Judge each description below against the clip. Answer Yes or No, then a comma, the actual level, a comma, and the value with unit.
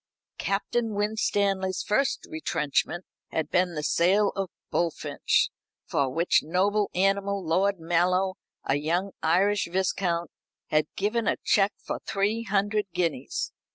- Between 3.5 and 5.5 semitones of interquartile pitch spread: No, average, 3.1 semitones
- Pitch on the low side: No, high, 190 Hz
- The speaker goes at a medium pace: No, slow, 120 wpm